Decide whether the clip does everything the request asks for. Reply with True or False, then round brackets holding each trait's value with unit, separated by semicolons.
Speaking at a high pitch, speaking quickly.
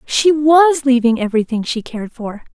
False (260 Hz; 165 wpm)